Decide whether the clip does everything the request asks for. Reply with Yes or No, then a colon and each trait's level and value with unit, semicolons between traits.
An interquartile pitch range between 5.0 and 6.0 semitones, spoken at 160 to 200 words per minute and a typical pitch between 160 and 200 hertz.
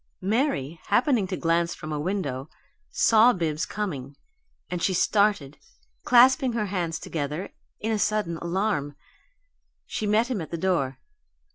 No: wide, 5.5 semitones; average, 140 wpm; medium, 185 Hz